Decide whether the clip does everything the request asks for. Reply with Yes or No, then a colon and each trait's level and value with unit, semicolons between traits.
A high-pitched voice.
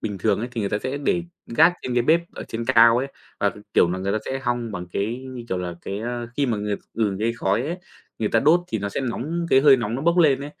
No: low, 120 Hz